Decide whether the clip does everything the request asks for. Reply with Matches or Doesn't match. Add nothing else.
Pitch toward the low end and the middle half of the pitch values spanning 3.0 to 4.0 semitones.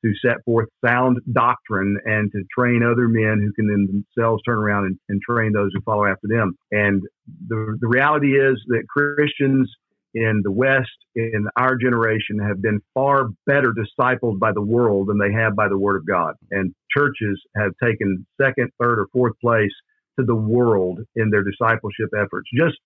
Matches